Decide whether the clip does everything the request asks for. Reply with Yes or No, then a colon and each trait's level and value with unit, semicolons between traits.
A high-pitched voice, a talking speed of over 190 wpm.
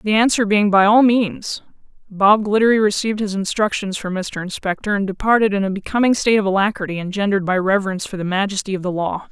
Yes: high, 200 Hz; average, 200 wpm